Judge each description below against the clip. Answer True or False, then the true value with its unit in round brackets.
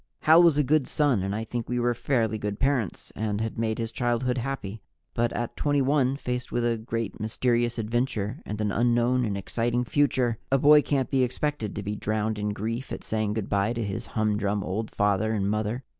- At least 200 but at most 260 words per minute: True (205 wpm)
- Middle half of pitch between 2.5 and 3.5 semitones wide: True (3.0 semitones)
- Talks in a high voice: False (115 Hz)